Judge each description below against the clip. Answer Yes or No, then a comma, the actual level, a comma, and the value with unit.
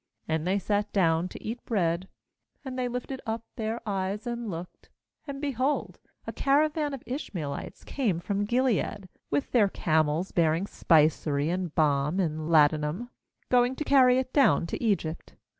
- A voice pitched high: Yes, high, 200 Hz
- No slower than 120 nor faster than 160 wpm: Yes, average, 155 wpm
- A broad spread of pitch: Yes, wide, 7.3 semitones